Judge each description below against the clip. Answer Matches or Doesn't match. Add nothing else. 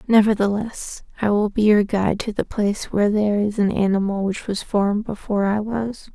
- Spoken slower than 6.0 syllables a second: Matches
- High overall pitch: Matches